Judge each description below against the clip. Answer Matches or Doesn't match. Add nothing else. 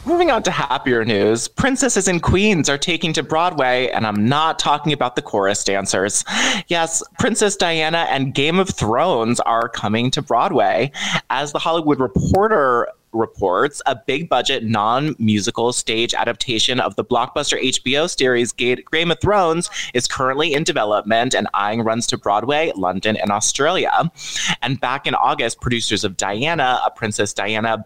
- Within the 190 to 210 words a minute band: Doesn't match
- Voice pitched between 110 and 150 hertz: Matches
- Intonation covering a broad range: Matches